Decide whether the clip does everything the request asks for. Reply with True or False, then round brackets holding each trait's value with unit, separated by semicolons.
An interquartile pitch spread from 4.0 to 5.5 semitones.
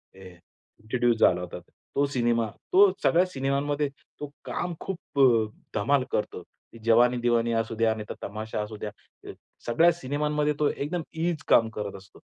True (5.2 semitones)